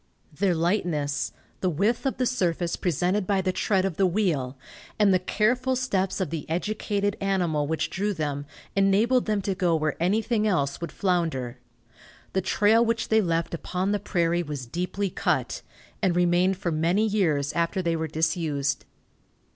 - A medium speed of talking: Yes, average, 165 wpm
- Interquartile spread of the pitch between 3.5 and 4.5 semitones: Yes, average, 4.0 semitones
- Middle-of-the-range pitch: Yes, medium, 180 Hz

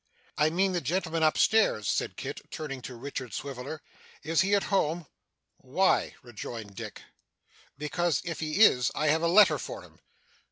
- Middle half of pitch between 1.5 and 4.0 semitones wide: No, average, 4.9 semitones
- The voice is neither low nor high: Yes, medium, 155 Hz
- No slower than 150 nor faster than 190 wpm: Yes, average, 165 wpm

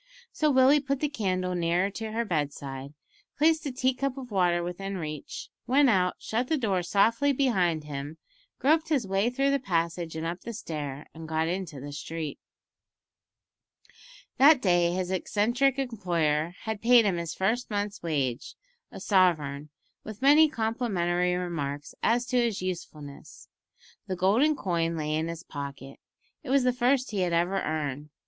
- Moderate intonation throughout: No, wide, 7.1 semitones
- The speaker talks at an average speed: Yes, average, 165 wpm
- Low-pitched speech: No, medium, 185 Hz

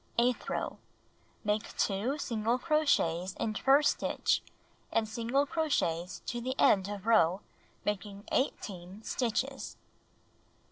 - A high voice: Yes, high, 220 Hz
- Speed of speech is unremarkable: No, slow, 110 wpm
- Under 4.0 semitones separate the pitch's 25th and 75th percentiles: No, average, 4.7 semitones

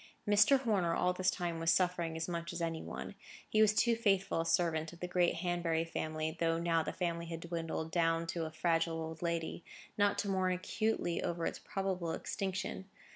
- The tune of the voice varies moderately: No, narrow, 2.1 semitones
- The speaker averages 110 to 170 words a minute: No, average, 195 wpm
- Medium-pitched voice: Yes, medium, 170 Hz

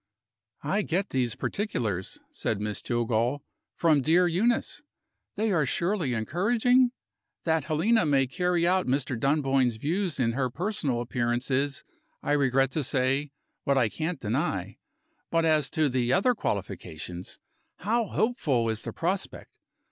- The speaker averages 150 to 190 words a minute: No, average, 140 wpm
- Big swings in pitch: Yes, wide, 6.6 semitones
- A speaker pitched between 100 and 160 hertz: Yes, medium, 140 Hz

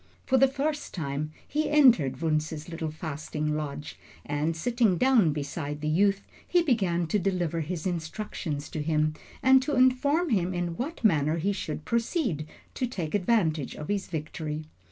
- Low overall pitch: No, medium, 170 Hz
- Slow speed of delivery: No, average, 160 wpm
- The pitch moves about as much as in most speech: No, wide, 7.4 semitones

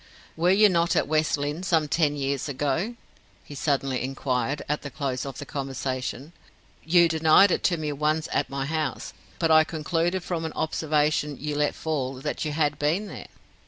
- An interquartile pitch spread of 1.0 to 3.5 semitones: Yes, narrow, 2.5 semitones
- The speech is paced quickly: No, average, 185 wpm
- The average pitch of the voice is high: No, medium, 150 Hz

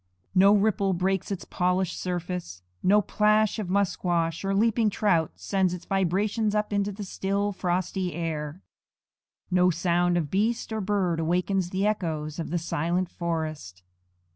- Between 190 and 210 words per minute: No, average, 145 wpm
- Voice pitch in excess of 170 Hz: Yes, medium, 185 Hz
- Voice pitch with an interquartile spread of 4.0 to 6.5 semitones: No, average, 2.9 semitones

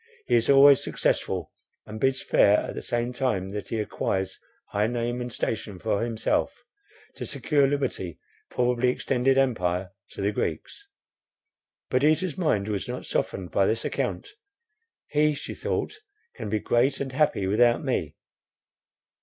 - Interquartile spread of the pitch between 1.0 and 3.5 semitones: No, average, 4.7 semitones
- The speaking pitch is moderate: No, low, 120 Hz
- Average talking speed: Yes, average, 145 wpm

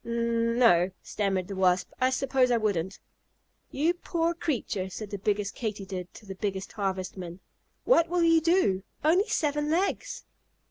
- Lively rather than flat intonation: Yes, wide, 7.8 semitones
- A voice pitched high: Yes, high, 220 Hz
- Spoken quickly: No, average, 150 wpm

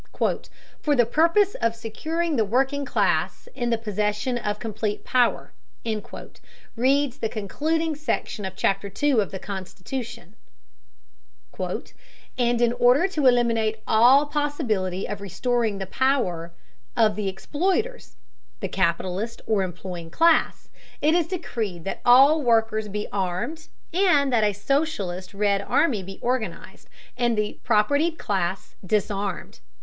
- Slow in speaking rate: Yes, slow, 130 wpm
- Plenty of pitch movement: Yes, wide, 5.8 semitones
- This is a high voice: Yes, high, 230 Hz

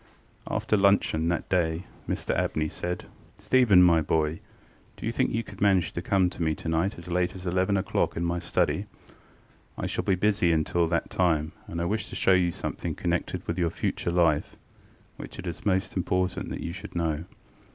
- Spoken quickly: No, average, 195 wpm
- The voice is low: Yes, very low, 85 Hz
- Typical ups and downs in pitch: No, narrow, 2.1 semitones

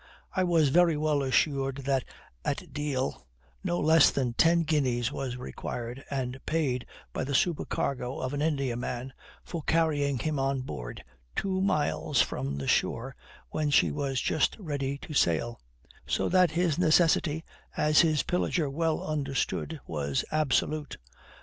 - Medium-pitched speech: Yes, medium, 145 Hz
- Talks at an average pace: Yes, average, 145 wpm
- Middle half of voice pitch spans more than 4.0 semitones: No, average, 3.4 semitones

